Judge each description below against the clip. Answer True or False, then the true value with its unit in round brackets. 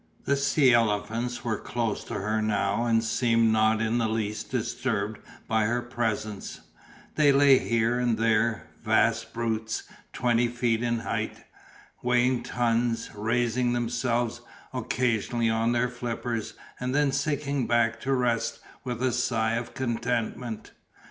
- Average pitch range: False (1.6 semitones)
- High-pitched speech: False (115 Hz)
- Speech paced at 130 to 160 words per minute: True (135 wpm)